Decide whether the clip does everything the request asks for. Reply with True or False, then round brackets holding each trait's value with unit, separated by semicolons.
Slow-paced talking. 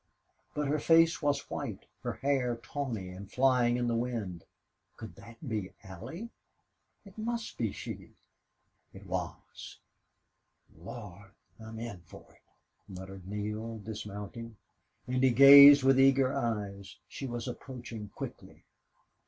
True (130 wpm)